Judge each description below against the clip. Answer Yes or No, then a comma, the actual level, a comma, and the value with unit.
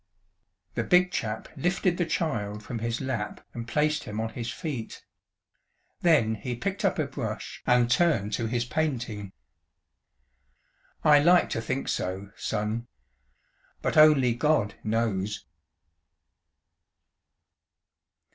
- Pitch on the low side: Yes, low, 120 Hz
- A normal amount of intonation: No, wide, 6.0 semitones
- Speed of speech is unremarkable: No, slow, 120 wpm